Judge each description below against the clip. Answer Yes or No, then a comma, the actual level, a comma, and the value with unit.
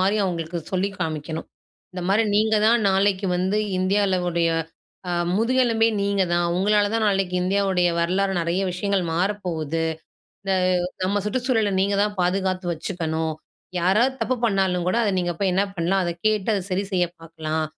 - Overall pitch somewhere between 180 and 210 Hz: Yes, high, 190 Hz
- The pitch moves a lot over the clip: No, average, 2.7 semitones